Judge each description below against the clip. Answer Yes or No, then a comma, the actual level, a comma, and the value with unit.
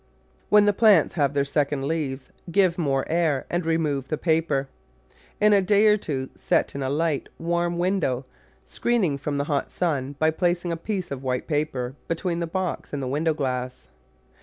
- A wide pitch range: No, average, 3.9 semitones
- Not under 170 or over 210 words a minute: Yes, average, 185 wpm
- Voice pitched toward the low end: No, medium, 160 Hz